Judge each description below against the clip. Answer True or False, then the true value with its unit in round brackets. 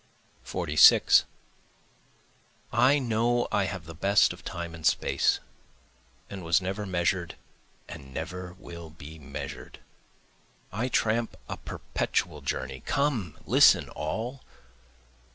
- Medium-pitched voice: False (90 Hz)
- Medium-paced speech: False (110 wpm)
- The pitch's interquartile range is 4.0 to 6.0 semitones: True (5.5 semitones)